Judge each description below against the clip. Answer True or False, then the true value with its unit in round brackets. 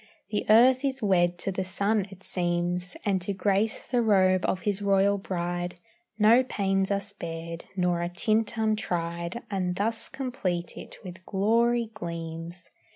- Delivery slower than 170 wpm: True (155 wpm)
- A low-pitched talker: False (195 Hz)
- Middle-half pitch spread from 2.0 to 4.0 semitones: True (3.5 semitones)